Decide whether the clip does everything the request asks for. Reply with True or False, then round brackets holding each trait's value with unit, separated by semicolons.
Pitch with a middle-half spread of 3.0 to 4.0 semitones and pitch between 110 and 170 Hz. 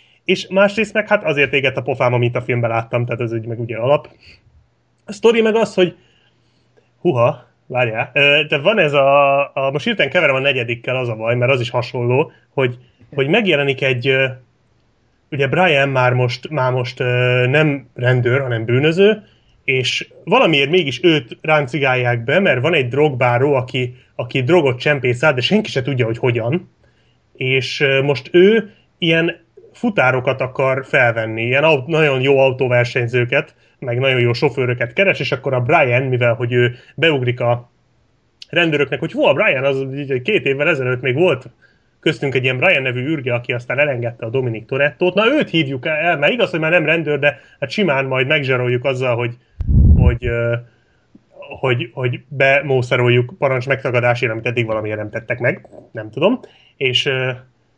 True (3.6 semitones; 130 Hz)